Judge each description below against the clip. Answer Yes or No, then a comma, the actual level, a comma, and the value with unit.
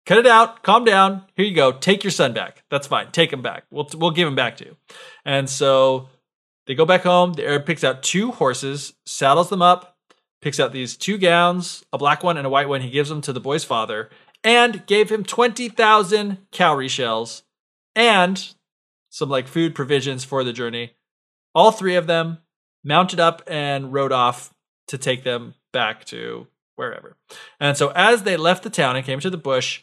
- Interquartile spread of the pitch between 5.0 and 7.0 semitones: Yes, wide, 5.6 semitones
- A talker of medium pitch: Yes, medium, 165 Hz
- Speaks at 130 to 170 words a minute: No, average, 200 wpm